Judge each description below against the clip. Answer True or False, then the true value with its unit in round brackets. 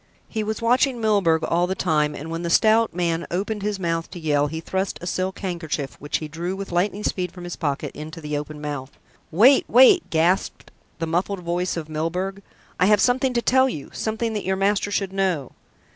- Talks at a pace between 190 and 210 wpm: True (205 wpm)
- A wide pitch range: False (4.2 semitones)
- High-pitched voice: False (180 Hz)